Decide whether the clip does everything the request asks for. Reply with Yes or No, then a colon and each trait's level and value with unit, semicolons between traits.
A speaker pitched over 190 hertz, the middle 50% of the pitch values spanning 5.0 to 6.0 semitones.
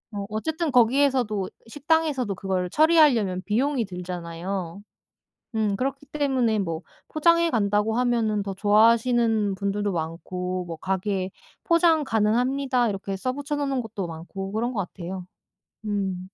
Yes: high, 215 Hz; wide, 5.4 semitones